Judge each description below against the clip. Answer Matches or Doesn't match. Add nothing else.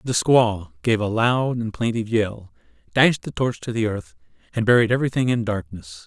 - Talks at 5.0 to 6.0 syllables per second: Matches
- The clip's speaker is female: Doesn't match